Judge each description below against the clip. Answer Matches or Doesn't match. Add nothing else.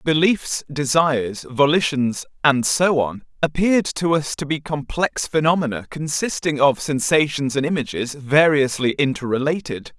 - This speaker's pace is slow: Matches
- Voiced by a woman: Doesn't match